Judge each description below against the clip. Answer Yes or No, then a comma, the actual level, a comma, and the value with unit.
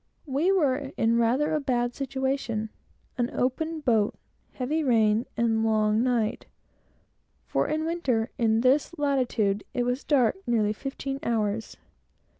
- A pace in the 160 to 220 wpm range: No, average, 140 wpm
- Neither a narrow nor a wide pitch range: Yes, average, 3.8 semitones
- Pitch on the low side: No, high, 245 Hz